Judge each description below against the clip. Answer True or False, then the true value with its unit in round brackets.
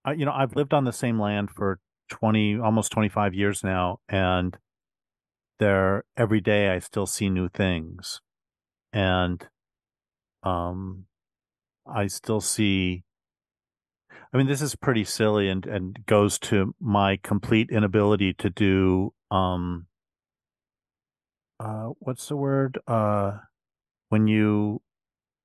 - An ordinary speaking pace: False (120 wpm)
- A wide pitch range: False (2.6 semitones)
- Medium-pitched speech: False (105 Hz)